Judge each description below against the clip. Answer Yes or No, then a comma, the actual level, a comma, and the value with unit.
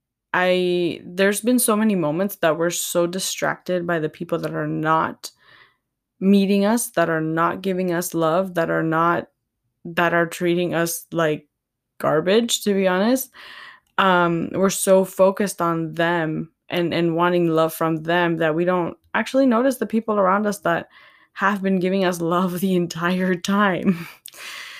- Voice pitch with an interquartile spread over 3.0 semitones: No, narrow, 2.6 semitones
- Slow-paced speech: No, average, 160 wpm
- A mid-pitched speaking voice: Yes, medium, 175 Hz